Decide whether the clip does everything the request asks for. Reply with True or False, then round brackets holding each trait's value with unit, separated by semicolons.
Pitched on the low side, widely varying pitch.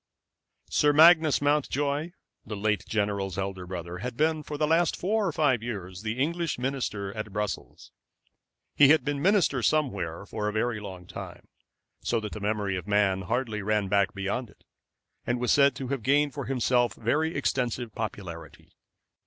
True (120 Hz; 6.1 semitones)